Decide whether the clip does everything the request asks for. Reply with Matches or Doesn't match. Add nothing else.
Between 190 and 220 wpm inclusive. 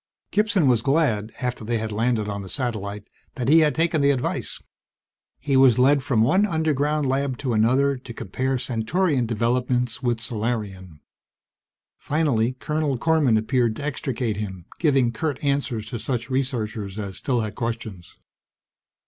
Doesn't match